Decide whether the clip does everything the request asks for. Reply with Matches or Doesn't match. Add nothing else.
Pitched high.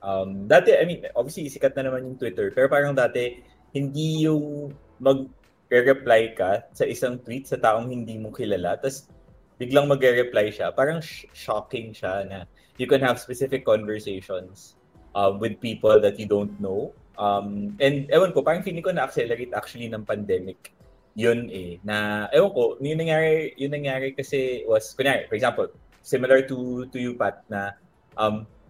Doesn't match